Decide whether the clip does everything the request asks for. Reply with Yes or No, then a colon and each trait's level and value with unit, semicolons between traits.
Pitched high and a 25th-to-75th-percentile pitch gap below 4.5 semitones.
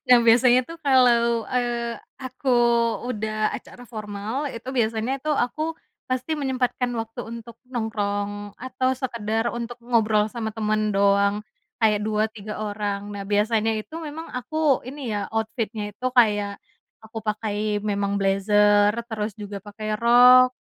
Yes: high, 225 Hz; average, 3.1 semitones